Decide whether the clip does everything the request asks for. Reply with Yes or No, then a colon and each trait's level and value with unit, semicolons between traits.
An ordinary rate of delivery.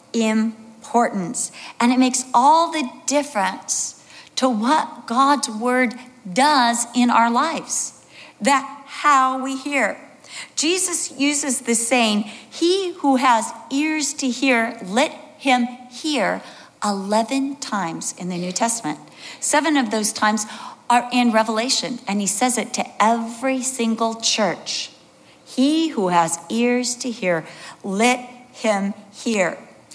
No: slow, 125 wpm